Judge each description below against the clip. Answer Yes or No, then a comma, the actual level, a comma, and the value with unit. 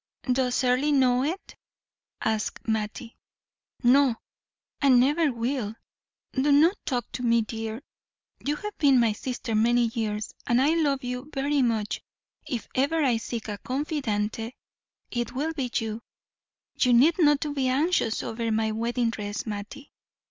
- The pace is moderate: Yes, average, 145 wpm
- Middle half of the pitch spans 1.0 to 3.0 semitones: No, average, 3.8 semitones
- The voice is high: Yes, very high, 250 Hz